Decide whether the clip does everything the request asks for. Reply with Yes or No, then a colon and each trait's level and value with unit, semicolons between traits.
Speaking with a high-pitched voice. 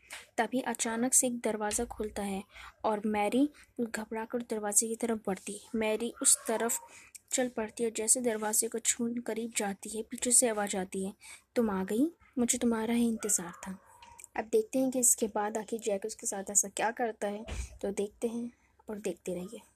Yes: high, 225 Hz